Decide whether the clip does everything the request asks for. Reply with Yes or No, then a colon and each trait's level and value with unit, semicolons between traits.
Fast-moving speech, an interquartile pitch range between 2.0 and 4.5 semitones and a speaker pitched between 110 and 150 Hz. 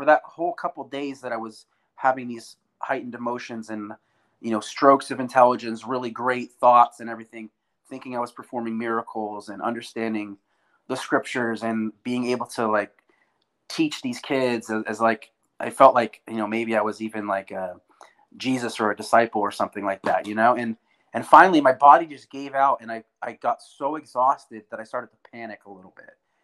No: average, 195 wpm; average, 2.8 semitones; low, 115 Hz